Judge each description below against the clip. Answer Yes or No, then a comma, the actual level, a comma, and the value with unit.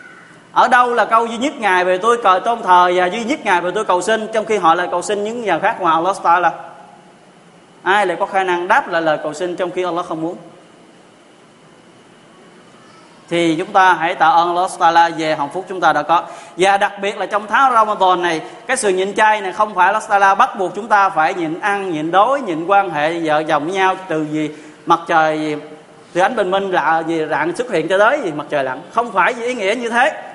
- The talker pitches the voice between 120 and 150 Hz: No, medium, 185 Hz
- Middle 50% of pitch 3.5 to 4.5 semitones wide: Yes, average, 4.1 semitones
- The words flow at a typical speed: Yes, average, 240 wpm